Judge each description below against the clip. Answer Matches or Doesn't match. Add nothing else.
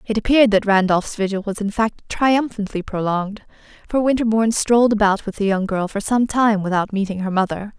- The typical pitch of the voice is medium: Doesn't match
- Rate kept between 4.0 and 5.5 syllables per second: Doesn't match